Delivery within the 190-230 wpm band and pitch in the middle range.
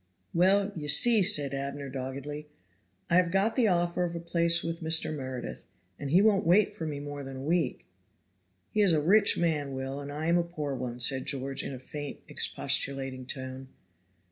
Yes: average, 195 wpm; medium, 150 Hz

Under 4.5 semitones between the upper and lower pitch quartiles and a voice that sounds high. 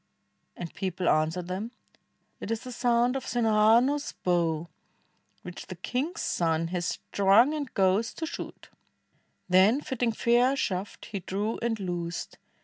No: average, 5.2 semitones; high, 210 Hz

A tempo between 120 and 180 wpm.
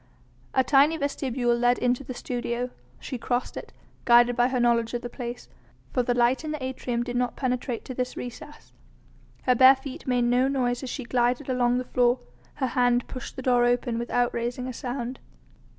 No: average, 195 wpm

